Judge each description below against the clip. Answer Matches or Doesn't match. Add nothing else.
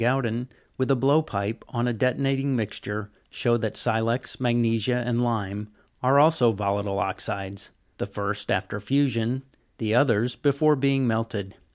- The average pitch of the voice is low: Matches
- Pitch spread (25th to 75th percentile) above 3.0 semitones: Matches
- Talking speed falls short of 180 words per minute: Matches